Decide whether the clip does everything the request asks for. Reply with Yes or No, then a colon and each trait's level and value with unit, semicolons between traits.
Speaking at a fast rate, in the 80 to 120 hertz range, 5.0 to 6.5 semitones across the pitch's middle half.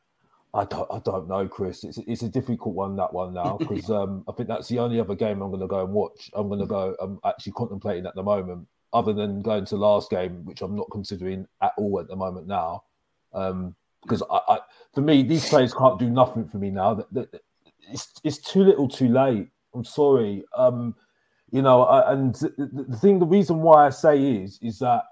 Yes: fast, 215 wpm; low, 115 Hz; average, 5.3 semitones